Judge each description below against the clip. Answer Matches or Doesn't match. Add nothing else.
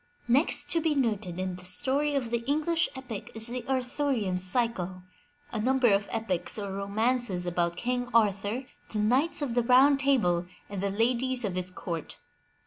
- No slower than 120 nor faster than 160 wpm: Doesn't match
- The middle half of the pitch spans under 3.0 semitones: Doesn't match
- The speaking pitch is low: Doesn't match